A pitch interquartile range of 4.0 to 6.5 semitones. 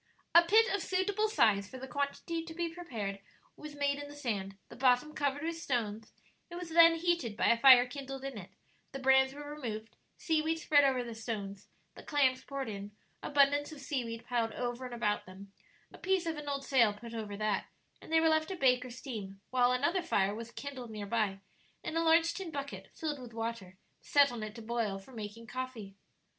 Yes: average, 5.2 semitones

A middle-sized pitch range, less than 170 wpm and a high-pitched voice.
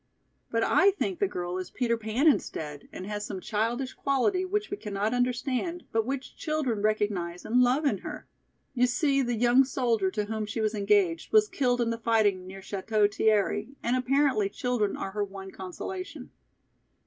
No: average, 4.4 semitones; average, 180 wpm; high, 230 Hz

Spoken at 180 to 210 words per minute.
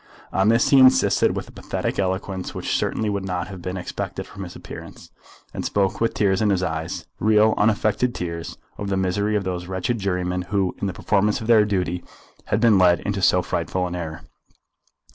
Yes: average, 200 wpm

